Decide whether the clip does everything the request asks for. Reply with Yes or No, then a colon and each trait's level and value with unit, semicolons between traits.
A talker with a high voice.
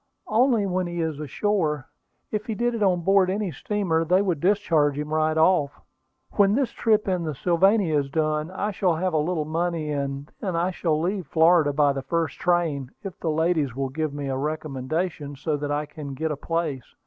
No: medium, 160 Hz